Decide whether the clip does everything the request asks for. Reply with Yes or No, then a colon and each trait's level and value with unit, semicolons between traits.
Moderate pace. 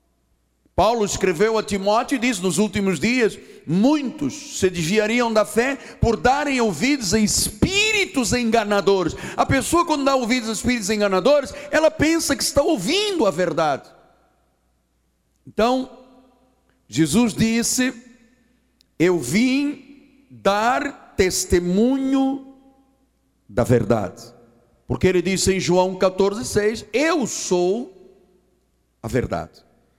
No: slow, 110 wpm